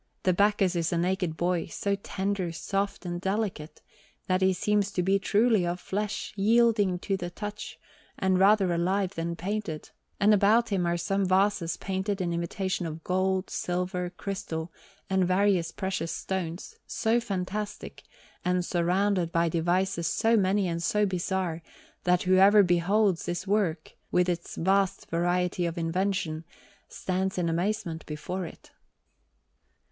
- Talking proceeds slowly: No, average, 145 wpm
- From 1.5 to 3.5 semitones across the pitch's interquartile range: Yes, narrow, 2.4 semitones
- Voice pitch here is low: No, medium, 185 Hz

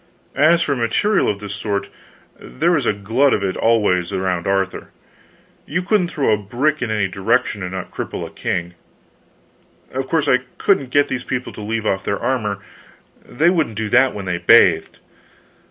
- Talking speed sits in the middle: Yes, average, 180 wpm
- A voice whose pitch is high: No, low, 115 Hz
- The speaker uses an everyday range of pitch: No, wide, 6.1 semitones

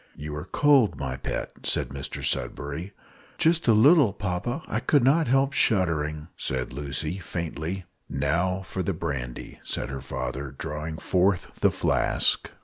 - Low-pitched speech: Yes, very low, 85 Hz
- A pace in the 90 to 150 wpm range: Yes, average, 145 wpm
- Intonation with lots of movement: Yes, wide, 6.6 semitones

